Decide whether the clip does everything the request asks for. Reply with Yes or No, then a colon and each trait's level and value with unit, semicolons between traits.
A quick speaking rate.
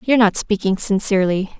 No: average, 150 wpm